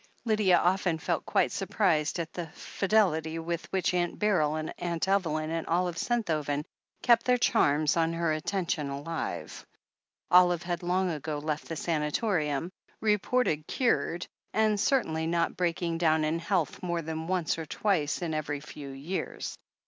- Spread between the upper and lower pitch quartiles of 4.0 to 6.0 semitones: No, average, 3.0 semitones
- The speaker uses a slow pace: No, average, 155 wpm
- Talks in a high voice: No, medium, 170 Hz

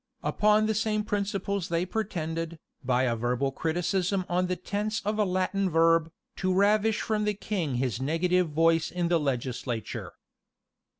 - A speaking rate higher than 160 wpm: No, average, 155 wpm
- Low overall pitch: No, medium, 180 Hz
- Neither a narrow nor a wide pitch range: Yes, average, 4.3 semitones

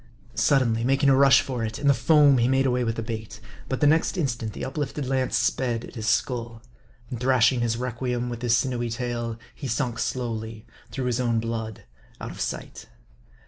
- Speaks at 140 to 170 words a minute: No, average, 200 wpm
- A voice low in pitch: Yes, low, 120 Hz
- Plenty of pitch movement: No, narrow, 2.5 semitones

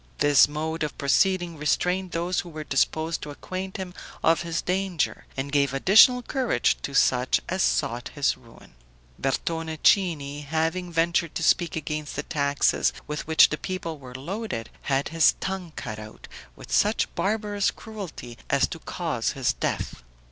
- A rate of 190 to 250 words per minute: No, average, 160 wpm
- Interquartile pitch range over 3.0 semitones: Yes, average, 4.5 semitones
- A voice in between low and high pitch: Yes, medium, 160 Hz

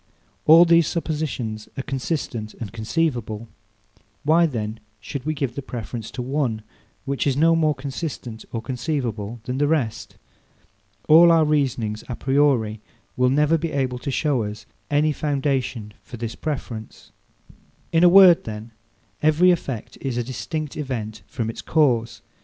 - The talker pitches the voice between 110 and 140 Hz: Yes, low, 135 Hz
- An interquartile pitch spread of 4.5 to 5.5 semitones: Yes, average, 5.0 semitones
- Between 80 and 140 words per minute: No, average, 150 wpm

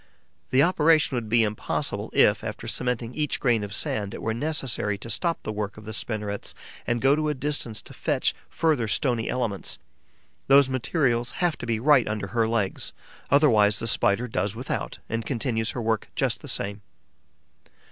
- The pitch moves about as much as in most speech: Yes, average, 4.0 semitones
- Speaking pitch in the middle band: No, low, 115 Hz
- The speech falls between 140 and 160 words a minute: No, average, 175 wpm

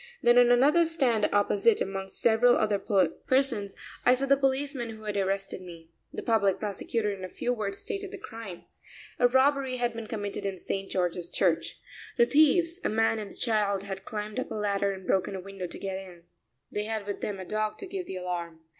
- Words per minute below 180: No, fast, 205 wpm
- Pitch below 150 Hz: No, high, 210 Hz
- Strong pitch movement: No, average, 4.1 semitones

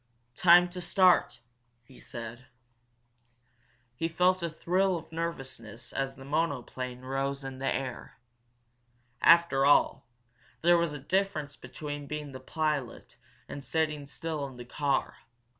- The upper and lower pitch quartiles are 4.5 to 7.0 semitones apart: No, average, 4.0 semitones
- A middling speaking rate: No, slow, 130 wpm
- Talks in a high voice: No, medium, 145 Hz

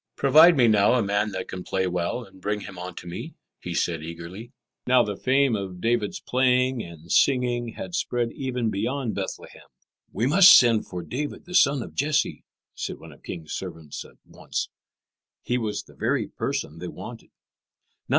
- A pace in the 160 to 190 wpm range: Yes, average, 170 wpm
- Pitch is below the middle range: Yes, low, 110 Hz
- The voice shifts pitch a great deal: Yes, wide, 5.8 semitones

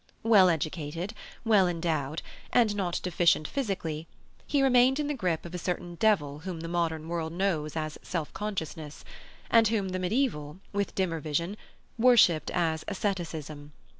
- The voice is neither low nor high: Yes, medium, 175 Hz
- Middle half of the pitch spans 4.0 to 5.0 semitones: Yes, average, 4.4 semitones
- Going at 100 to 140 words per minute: No, average, 150 wpm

